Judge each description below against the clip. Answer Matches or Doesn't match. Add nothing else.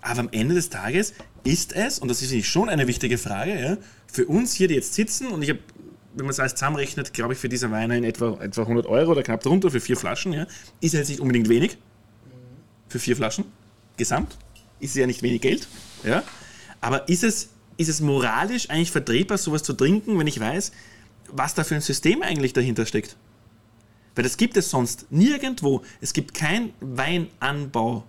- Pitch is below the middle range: Matches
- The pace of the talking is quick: Matches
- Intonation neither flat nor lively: Doesn't match